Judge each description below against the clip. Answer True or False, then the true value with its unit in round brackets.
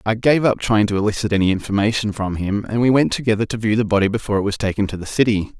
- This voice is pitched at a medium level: False (105 Hz)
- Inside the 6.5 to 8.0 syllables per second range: True (7.0 syllables/s)